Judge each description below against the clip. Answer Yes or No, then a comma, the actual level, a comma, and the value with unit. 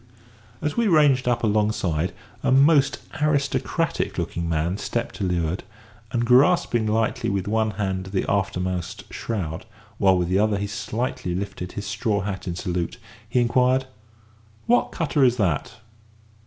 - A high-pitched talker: No, low, 105 Hz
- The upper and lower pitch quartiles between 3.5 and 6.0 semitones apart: Yes, average, 5.2 semitones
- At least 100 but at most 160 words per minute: Yes, average, 145 wpm